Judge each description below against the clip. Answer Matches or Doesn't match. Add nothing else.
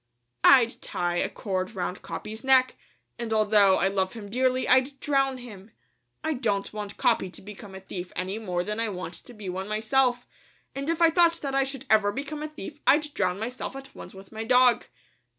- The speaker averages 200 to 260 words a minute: Matches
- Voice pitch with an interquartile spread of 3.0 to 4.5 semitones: Doesn't match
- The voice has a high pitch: Matches